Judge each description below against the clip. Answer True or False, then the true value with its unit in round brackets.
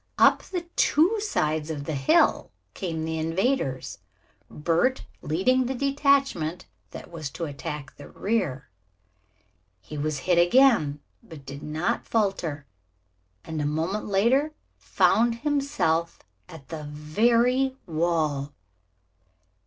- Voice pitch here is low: False (170 Hz)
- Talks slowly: True (115 wpm)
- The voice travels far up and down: True (8.2 semitones)